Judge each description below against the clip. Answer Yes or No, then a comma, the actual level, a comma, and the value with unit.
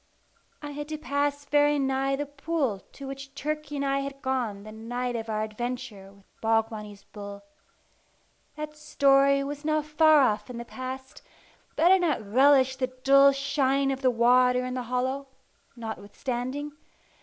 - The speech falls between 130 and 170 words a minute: Yes, average, 165 wpm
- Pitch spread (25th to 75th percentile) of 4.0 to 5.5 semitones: No, average, 3.0 semitones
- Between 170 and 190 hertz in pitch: No, very high, 265 Hz